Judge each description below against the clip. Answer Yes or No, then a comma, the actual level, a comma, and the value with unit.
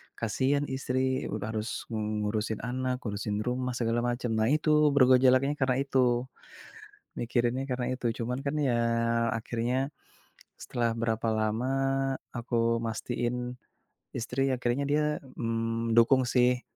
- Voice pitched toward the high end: No, low, 125 Hz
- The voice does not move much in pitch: Yes, narrow, 2.2 semitones